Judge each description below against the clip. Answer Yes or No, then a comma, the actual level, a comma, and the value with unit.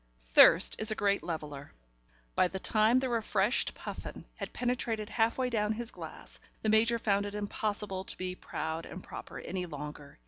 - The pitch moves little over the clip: No, average, 3.6 semitones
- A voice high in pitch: Yes, high, 205 Hz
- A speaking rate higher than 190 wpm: No, average, 175 wpm